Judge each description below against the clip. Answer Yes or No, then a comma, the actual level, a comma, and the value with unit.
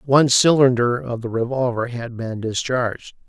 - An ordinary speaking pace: Yes, average, 145 wpm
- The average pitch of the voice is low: Yes, low, 125 Hz